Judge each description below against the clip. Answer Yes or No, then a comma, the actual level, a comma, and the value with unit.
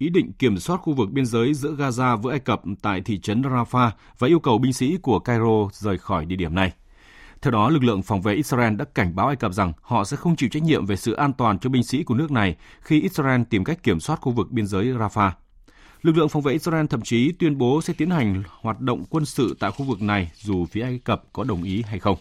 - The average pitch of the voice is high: No, low, 120 Hz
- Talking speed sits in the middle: No, fast, 265 wpm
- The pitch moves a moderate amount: No, wide, 5.9 semitones